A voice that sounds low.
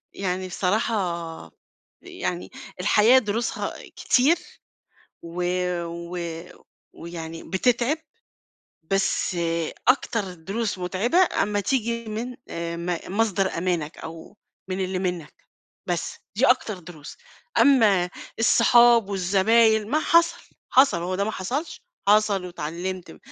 No: high, 195 Hz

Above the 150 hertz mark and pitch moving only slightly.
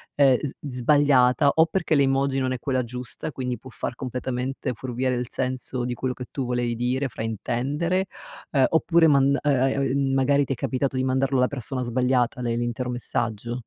No: low, 130 Hz; narrow, 1.9 semitones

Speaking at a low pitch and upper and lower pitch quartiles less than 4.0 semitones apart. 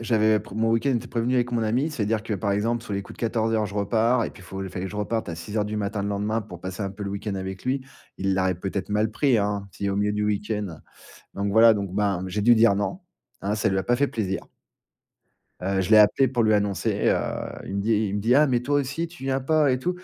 Yes: low, 105 Hz; average, 2.8 semitones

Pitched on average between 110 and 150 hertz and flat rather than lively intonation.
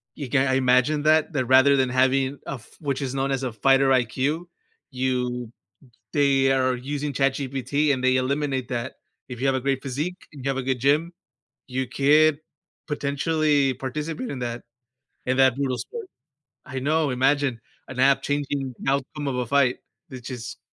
Yes: low, 135 Hz; narrow, 1.9 semitones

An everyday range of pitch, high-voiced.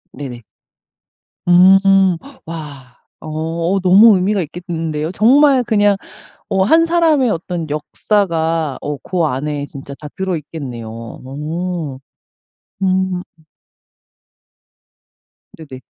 No: average, 4.5 semitones; medium, 170 Hz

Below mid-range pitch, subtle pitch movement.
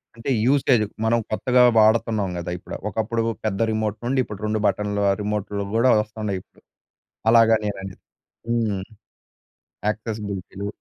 Yes: low, 105 Hz; narrow, 2.1 semitones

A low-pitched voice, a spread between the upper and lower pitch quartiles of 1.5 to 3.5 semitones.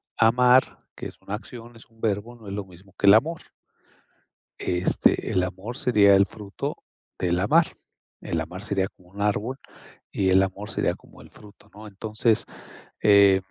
Yes: low, 100 Hz; average, 2.8 semitones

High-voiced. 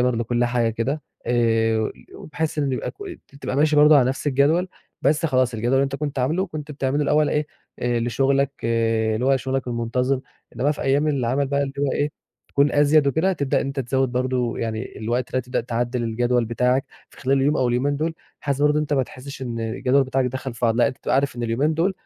No: low, 130 Hz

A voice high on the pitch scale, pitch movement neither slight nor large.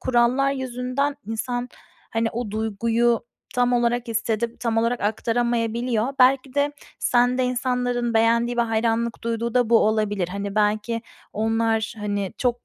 No: high, 235 Hz; narrow, 1.8 semitones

